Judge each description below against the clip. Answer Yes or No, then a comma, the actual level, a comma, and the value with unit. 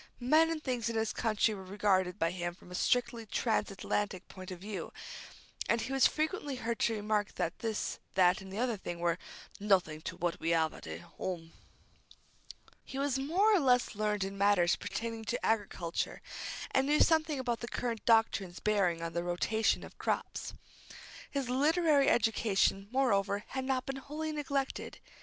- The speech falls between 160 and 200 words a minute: Yes, average, 175 wpm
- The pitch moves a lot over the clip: Yes, wide, 5.9 semitones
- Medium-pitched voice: No, high, 220 Hz